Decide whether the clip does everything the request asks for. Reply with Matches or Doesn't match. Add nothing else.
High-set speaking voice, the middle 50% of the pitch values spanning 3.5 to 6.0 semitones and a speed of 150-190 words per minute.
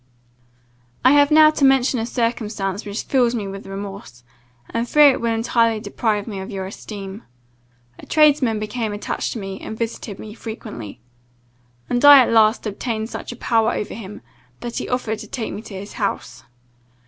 Doesn't match